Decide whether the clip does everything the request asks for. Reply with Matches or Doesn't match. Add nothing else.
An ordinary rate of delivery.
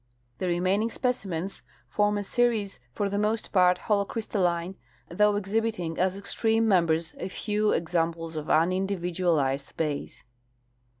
Doesn't match